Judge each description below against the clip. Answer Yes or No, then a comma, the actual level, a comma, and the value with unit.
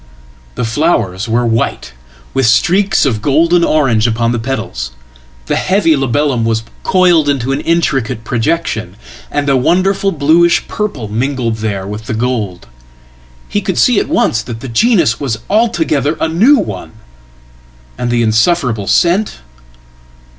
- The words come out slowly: Yes, slow, 130 wpm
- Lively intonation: Yes, wide, 7.1 semitones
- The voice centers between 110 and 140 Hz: Yes, low, 135 Hz